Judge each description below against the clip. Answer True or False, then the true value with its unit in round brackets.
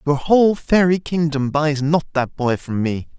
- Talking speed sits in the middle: True (190 wpm)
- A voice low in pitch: False (150 Hz)